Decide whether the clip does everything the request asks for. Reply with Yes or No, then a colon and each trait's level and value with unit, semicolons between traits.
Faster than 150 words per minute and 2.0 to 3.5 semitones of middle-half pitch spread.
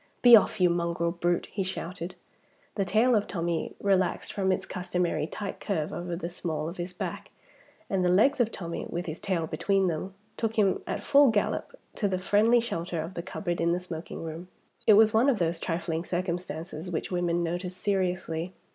Yes: average, 190 wpm; average, 2.7 semitones